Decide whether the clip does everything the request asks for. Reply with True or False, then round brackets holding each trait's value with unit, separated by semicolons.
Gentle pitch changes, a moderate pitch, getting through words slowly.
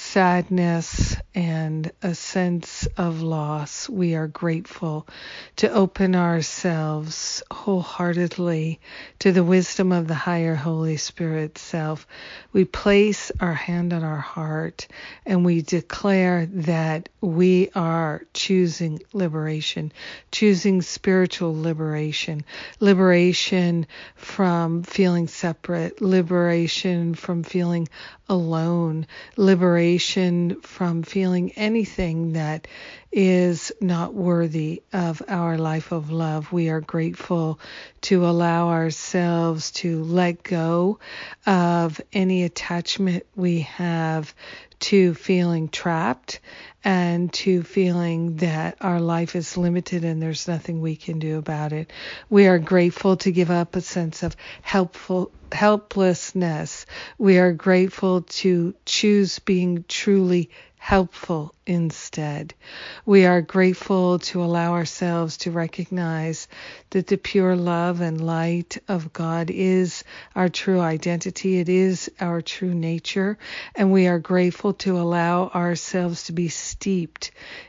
True (2.0 semitones; 175 Hz; 115 wpm)